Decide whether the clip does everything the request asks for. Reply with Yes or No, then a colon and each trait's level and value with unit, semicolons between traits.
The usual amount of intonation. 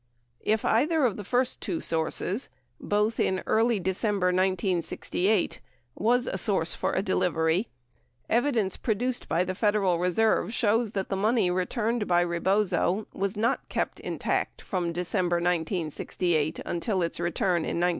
Yes: average, 3.8 semitones